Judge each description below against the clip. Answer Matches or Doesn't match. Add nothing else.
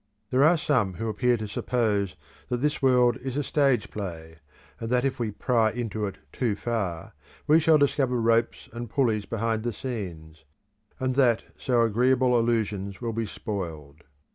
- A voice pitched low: Matches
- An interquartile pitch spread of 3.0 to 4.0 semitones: Matches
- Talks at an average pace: Matches